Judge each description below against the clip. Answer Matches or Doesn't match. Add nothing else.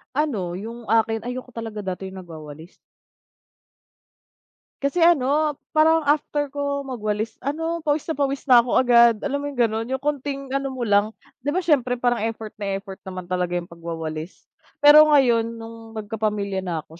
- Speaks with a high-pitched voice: Matches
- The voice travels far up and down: Matches